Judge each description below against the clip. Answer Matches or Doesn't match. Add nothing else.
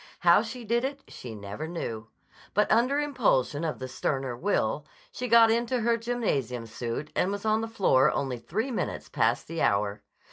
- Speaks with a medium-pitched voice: Matches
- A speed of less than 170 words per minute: Doesn't match